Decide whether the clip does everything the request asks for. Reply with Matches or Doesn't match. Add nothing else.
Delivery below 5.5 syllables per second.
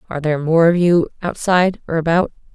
Doesn't match